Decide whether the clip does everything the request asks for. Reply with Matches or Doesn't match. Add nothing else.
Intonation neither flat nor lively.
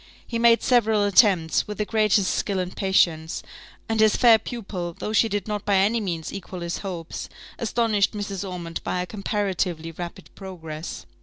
Matches